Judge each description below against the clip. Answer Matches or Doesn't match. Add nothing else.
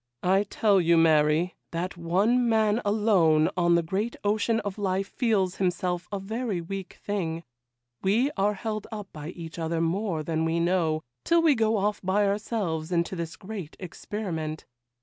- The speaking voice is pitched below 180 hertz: Doesn't match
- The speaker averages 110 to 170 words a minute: Matches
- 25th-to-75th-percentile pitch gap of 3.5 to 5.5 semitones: Matches